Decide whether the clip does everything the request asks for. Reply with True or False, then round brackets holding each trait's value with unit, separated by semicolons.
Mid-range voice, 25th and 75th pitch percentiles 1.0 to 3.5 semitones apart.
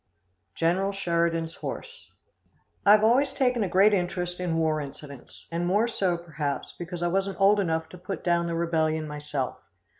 True (175 Hz; 3.2 semitones)